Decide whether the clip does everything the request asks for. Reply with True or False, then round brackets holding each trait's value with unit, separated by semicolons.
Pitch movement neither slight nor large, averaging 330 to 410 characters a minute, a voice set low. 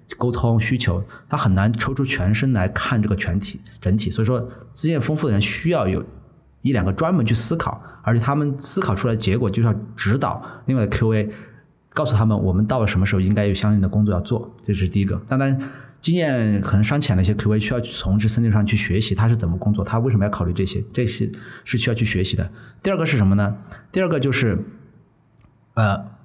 True (3.4 semitones; 335 characters per minute; 110 Hz)